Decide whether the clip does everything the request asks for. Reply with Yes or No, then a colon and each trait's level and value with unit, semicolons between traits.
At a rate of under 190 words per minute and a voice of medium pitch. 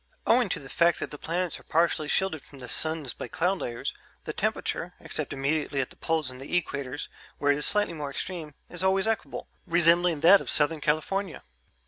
No: average, 200 wpm; medium, 160 Hz